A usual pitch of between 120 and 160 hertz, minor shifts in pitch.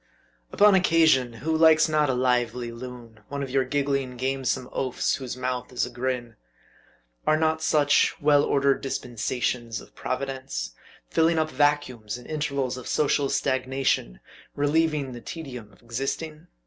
No: low, 135 Hz; average, 3.2 semitones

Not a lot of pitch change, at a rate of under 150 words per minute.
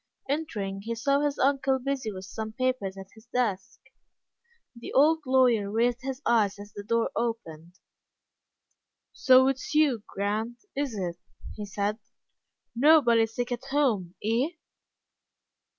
No: average, 4.4 semitones; slow, 135 wpm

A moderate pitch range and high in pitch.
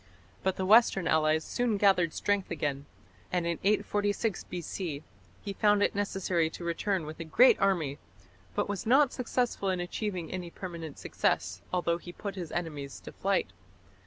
No: average, 3.7 semitones; medium, 180 Hz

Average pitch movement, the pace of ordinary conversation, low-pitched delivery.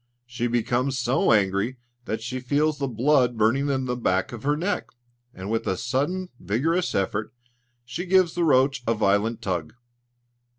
Yes: average, 4.4 semitones; average, 165 wpm; low, 125 Hz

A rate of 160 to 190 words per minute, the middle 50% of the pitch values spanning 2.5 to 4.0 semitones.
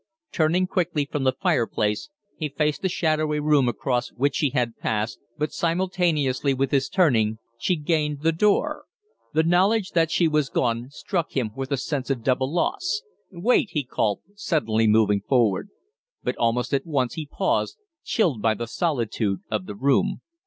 No: average, 165 wpm; wide, 5.6 semitones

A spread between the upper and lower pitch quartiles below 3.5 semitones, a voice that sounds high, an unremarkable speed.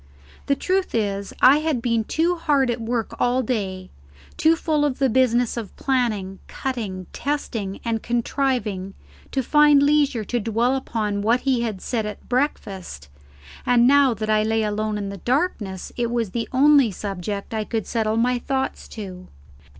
No: average, 4.1 semitones; high, 235 Hz; average, 165 wpm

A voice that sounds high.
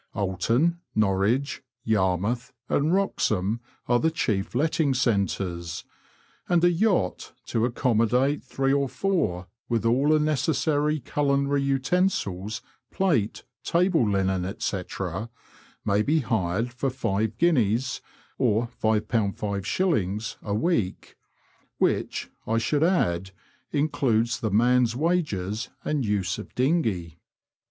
No: low, 120 Hz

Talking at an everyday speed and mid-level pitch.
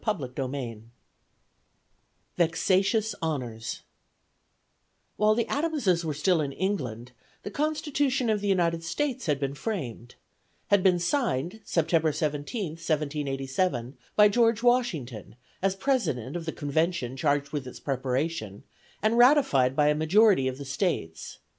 No: slow, 130 wpm; medium, 165 Hz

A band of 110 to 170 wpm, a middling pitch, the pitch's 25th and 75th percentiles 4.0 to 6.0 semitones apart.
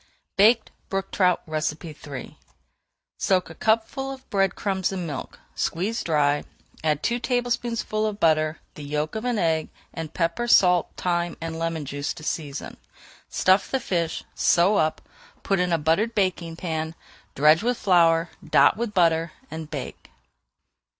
Yes: average, 150 wpm; medium, 170 Hz; average, 4.6 semitones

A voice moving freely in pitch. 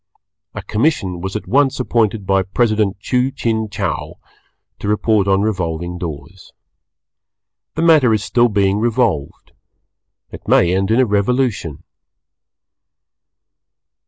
No: average, 3.8 semitones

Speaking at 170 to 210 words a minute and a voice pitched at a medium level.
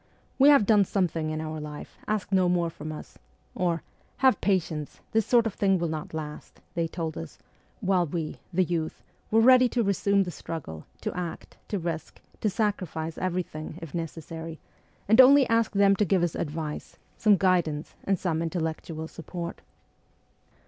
Yes: average, 175 wpm; medium, 175 Hz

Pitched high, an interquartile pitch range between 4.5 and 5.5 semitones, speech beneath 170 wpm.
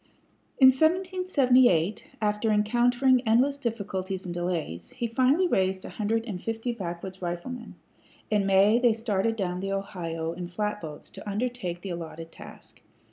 Yes: high, 210 Hz; average, 5.1 semitones; average, 140 wpm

